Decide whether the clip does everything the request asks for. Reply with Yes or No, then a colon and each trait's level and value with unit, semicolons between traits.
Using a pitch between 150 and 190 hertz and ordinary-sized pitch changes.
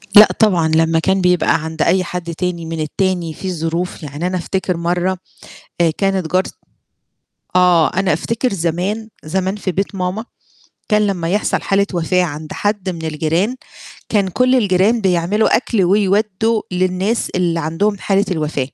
Yes: medium, 185 Hz; average, 3.1 semitones